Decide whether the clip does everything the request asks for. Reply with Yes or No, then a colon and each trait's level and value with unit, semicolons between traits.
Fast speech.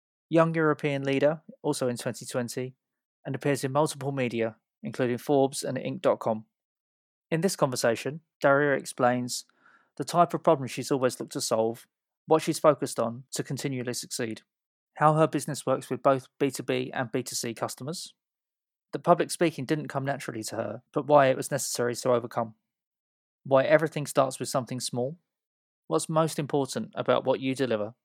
No: average, 160 wpm